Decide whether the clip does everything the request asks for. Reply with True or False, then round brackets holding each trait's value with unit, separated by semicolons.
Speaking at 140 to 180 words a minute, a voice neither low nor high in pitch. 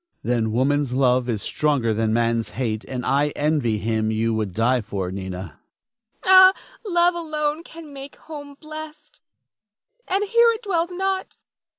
True (155 wpm; 145 Hz)